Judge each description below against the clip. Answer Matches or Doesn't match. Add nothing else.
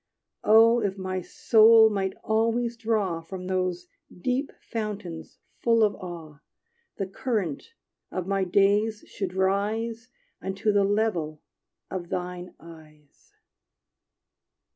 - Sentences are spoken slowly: Matches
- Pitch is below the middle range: Doesn't match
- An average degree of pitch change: Matches